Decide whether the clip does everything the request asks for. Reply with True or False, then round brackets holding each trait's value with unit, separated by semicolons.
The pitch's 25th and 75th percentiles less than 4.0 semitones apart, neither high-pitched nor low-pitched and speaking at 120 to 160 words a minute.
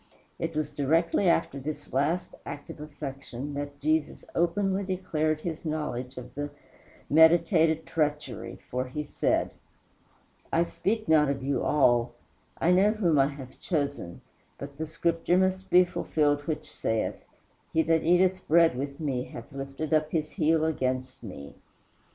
True (3.1 semitones; 155 Hz; 150 wpm)